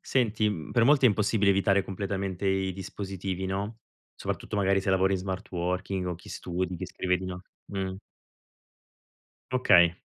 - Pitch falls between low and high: No, very low, 95 Hz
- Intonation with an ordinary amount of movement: No, narrow, 1.6 semitones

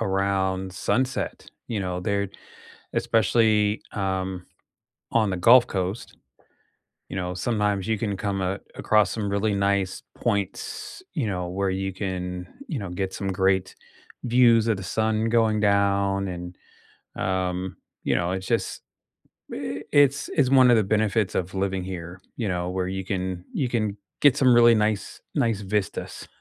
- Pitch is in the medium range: No, low, 100 Hz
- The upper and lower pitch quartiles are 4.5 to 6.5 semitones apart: No, average, 2.7 semitones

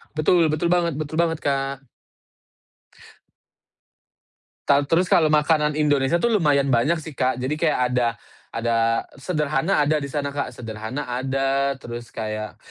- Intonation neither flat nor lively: Yes, average, 3.4 semitones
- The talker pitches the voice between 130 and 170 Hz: Yes, medium, 140 Hz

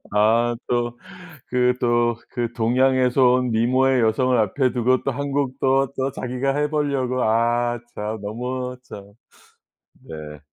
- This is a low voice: Yes, low, 125 Hz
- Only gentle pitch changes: Yes, narrow, 1.9 semitones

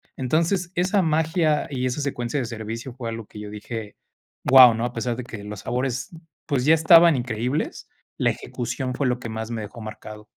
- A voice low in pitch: Yes, low, 125 Hz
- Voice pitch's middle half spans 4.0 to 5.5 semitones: Yes, average, 4.8 semitones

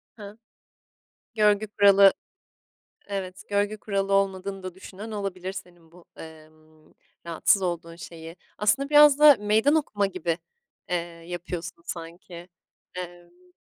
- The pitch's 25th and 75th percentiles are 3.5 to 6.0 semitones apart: No, average, 2.9 semitones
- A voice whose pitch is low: No, medium, 185 Hz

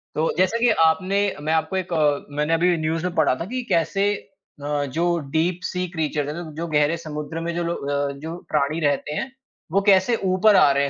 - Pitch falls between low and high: Yes, medium, 160 Hz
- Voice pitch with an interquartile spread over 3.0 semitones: Yes, average, 3.4 semitones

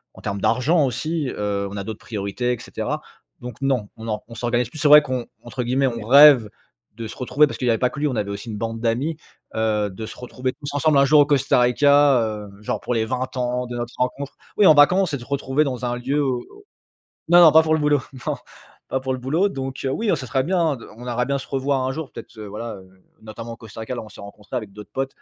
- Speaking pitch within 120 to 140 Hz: Yes, low, 125 Hz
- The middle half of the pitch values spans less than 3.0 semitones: No, average, 3.9 semitones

